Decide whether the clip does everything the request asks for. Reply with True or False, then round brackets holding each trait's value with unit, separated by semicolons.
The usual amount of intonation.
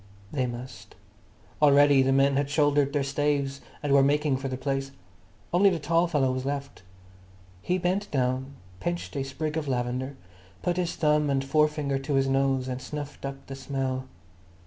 False (1.9 semitones)